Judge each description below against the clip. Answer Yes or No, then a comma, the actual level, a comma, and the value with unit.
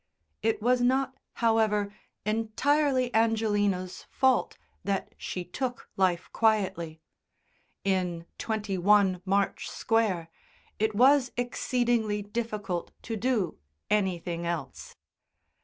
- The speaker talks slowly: Yes, slow, 90 wpm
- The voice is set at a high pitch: Yes, high, 210 Hz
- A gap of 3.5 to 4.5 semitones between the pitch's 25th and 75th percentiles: Yes, average, 3.8 semitones